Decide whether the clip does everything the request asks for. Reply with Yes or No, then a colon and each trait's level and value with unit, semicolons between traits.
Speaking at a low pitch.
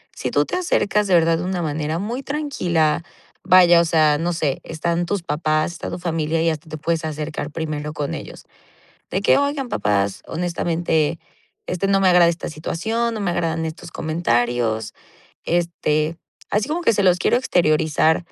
No: medium, 165 Hz